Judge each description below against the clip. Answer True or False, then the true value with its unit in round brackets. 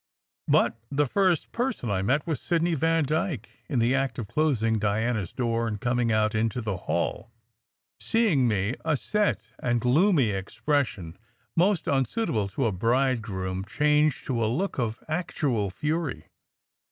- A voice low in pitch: True (125 Hz)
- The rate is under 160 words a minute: True (150 wpm)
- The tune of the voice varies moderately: False (6.0 semitones)